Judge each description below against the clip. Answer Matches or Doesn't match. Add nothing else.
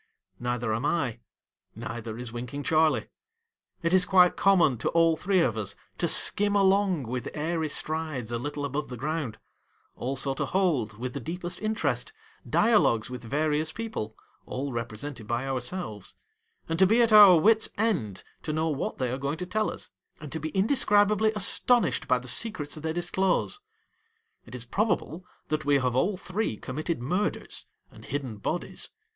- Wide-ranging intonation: Matches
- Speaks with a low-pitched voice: Doesn't match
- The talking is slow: Doesn't match